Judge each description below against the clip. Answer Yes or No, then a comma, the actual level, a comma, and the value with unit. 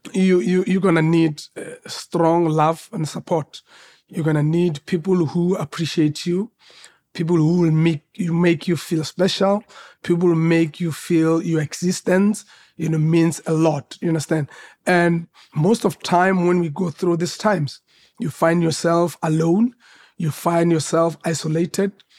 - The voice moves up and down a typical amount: No, narrow, 2.2 semitones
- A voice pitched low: No, medium, 170 Hz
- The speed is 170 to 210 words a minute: No, average, 155 wpm